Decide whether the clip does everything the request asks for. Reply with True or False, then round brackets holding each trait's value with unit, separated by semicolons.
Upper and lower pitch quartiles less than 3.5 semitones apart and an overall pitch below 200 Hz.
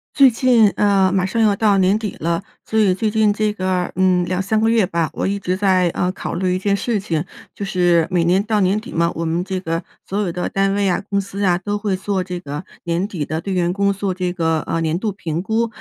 True (2.5 semitones; 190 Hz)